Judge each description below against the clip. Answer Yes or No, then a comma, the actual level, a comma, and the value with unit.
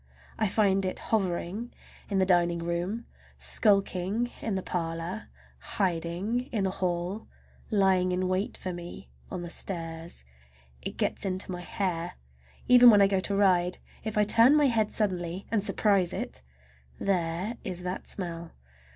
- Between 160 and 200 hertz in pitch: Yes, medium, 185 Hz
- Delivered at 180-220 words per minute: No, average, 150 wpm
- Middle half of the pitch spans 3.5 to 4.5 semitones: No, average, 3.1 semitones